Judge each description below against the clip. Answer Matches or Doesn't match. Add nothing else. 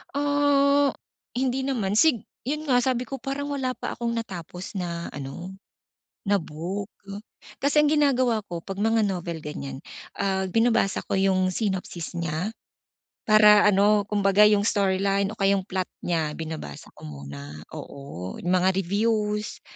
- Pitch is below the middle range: Doesn't match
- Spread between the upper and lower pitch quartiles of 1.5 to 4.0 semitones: Doesn't match